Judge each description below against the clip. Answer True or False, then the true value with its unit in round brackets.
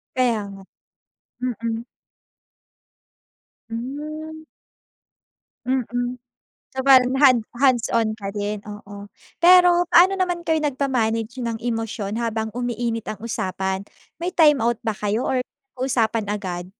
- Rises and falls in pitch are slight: False (3.6 semitones)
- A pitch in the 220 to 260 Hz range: True (235 Hz)